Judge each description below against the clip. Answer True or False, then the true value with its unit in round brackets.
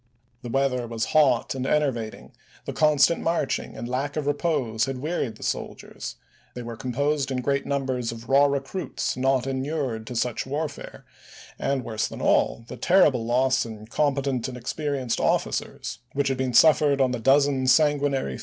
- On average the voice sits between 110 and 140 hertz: True (135 Hz)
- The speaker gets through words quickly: False (170 wpm)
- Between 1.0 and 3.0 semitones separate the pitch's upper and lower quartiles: True (2.7 semitones)